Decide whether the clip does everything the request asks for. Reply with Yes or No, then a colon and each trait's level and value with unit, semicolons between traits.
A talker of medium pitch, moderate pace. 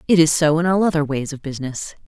No: medium, 155 Hz; fast, 260 wpm